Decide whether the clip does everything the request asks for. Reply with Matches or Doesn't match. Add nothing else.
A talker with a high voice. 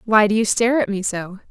Matches